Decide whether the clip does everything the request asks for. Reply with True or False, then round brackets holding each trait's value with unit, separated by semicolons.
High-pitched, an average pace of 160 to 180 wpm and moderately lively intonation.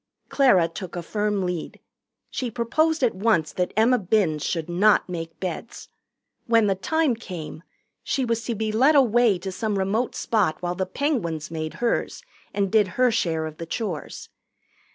True (205 Hz; 170 wpm; 5.0 semitones)